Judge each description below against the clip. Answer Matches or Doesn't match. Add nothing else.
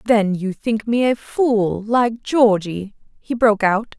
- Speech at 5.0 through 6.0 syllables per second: Doesn't match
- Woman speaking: Matches